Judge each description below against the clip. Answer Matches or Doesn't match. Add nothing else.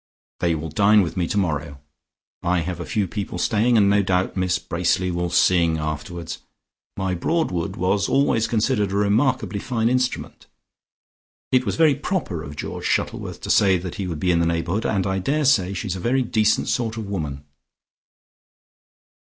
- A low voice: Matches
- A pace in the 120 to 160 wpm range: Doesn't match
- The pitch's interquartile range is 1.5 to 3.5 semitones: Doesn't match